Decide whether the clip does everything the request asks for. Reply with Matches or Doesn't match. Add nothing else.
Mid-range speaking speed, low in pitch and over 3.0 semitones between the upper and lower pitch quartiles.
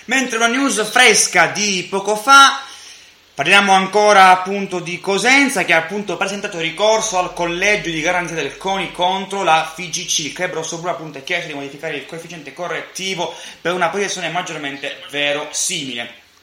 Doesn't match